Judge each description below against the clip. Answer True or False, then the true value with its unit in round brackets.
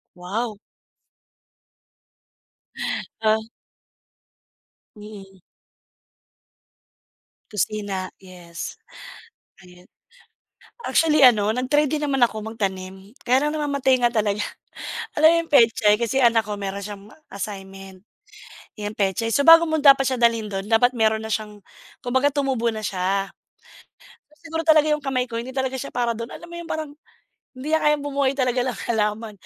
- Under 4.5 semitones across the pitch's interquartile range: False (4.9 semitones)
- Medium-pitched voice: False (230 Hz)